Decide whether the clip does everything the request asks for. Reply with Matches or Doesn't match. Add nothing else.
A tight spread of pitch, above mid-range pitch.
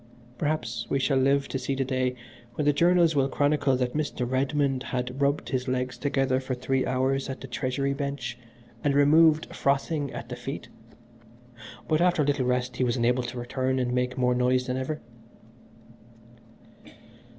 Doesn't match